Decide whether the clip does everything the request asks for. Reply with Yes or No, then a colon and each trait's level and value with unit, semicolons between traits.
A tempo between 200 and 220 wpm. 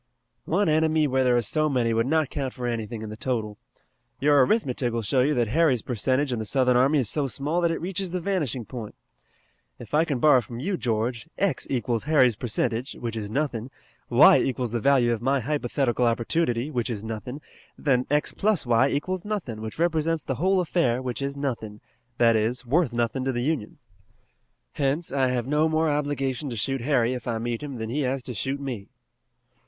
Yes: fast, 205 wpm